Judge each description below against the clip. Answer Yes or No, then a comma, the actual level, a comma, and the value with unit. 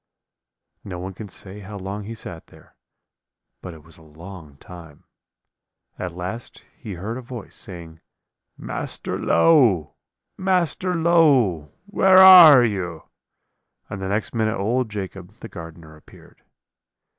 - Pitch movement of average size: No, wide, 6.0 semitones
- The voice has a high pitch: No, low, 100 Hz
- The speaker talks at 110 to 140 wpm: Yes, slow, 135 wpm